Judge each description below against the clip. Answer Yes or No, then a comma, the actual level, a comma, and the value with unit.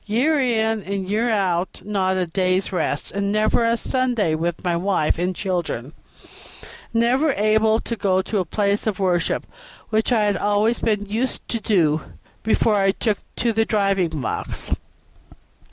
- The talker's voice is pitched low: No, high, 205 Hz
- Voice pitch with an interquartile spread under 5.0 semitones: Yes, average, 3.2 semitones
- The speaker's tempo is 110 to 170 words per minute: Yes, average, 165 wpm